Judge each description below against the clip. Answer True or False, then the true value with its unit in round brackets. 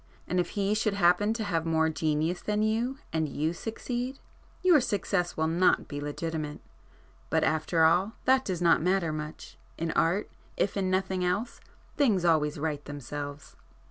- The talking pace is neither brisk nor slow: True (160 wpm)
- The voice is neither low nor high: True (175 Hz)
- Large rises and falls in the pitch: False (4.5 semitones)